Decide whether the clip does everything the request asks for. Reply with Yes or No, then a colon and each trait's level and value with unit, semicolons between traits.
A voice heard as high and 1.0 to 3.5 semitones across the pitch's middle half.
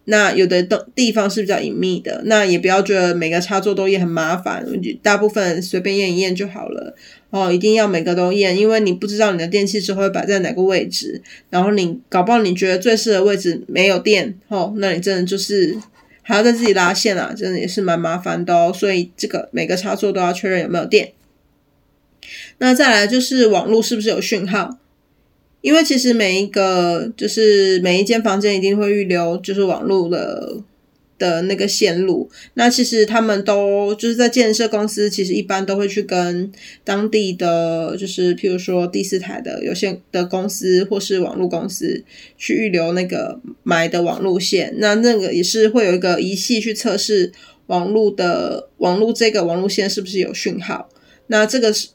Yes: high, 200 Hz; average, 2.9 semitones